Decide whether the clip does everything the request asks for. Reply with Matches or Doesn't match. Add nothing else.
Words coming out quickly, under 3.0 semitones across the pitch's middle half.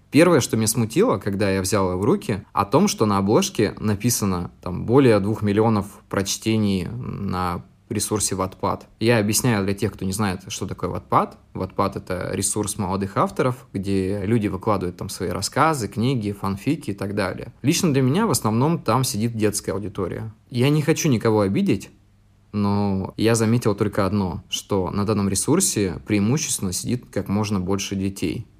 Matches